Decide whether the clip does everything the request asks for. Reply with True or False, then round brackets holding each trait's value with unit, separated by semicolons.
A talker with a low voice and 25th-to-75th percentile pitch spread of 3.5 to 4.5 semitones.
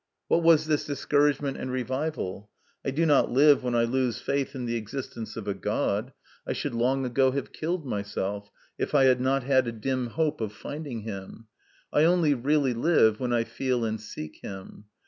True (130 Hz; 4.0 semitones)